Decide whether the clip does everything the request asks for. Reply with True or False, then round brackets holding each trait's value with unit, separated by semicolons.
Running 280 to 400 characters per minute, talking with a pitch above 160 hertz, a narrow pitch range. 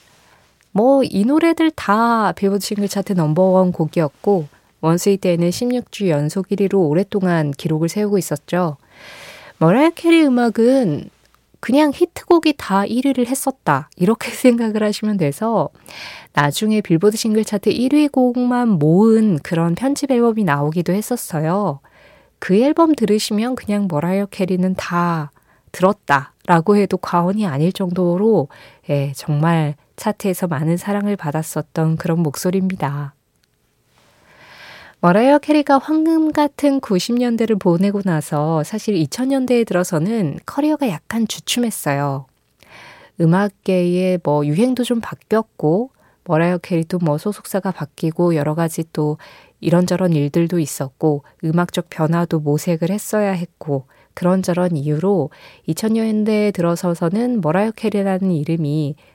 False (290 characters per minute; 185 Hz; 5.2 semitones)